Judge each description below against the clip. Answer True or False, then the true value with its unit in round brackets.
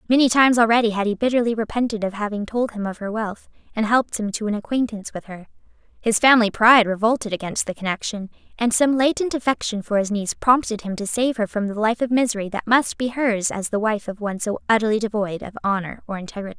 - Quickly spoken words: True (225 wpm)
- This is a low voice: False (220 Hz)